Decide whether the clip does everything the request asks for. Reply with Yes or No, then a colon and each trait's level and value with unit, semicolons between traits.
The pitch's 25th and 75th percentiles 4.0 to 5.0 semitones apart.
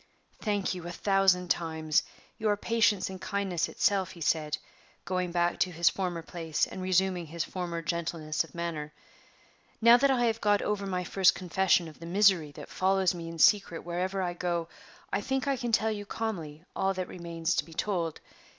No: average, 2.9 semitones